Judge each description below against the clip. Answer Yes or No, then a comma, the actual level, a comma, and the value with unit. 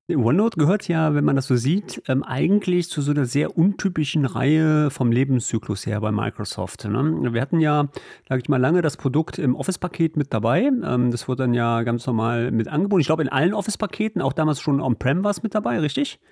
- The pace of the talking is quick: Yes, fast, 200 wpm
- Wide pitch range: Yes, wide, 5.8 semitones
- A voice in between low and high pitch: Yes, medium, 145 Hz